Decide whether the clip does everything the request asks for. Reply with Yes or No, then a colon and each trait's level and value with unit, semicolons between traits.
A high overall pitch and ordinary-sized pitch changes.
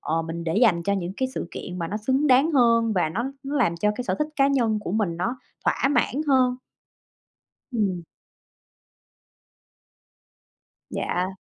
No: high, 220 Hz; wide, 6.6 semitones